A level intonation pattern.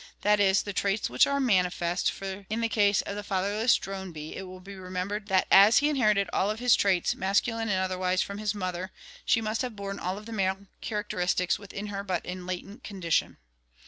Yes: narrow, 2.2 semitones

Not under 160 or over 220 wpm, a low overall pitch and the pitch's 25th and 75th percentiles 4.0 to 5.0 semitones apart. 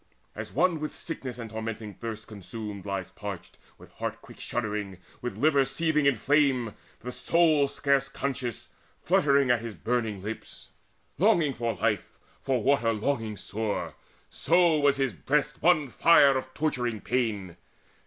No: average, 150 wpm; low, 125 Hz; average, 4.6 semitones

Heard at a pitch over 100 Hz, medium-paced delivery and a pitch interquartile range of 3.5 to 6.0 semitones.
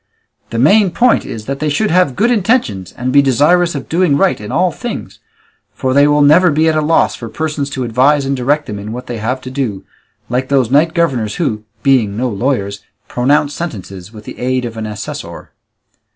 No: low, 135 Hz; fast, 210 wpm; average, 5.1 semitones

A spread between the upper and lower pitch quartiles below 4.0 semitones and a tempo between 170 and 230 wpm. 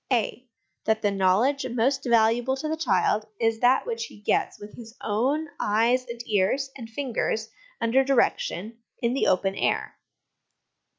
No: average, 3.5 semitones; average, 155 wpm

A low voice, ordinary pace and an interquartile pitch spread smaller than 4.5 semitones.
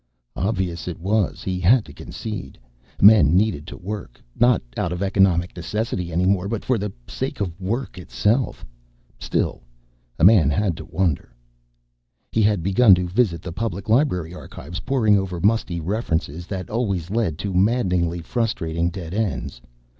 Yes: very low, 95 Hz; average, 155 wpm; average, 3.9 semitones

